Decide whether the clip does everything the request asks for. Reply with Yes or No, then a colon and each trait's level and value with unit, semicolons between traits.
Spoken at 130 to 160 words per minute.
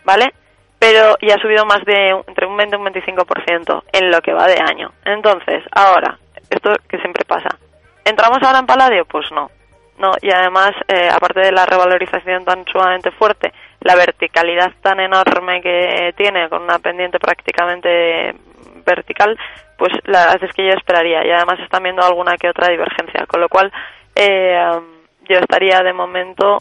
No: average, 170 wpm